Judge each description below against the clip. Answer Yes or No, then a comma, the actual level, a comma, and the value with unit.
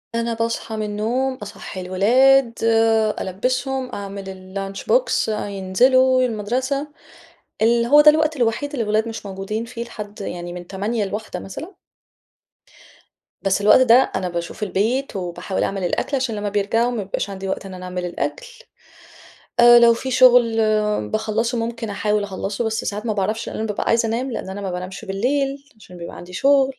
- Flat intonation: No, average, 4.1 semitones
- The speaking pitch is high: Yes, high, 220 Hz